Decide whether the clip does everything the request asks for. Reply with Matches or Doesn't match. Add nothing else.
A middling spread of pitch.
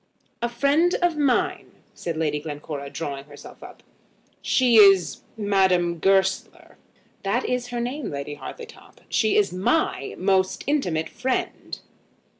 Doesn't match